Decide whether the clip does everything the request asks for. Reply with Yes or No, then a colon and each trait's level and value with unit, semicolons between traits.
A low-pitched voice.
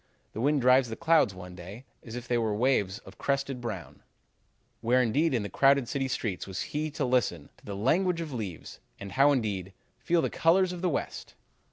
Yes: low, 125 Hz